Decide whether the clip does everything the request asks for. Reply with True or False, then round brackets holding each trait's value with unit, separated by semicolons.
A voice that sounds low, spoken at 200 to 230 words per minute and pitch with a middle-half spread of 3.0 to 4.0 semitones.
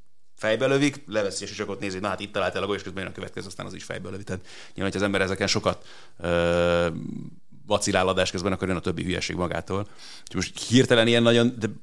False (95 Hz; 215 wpm; 2.4 semitones)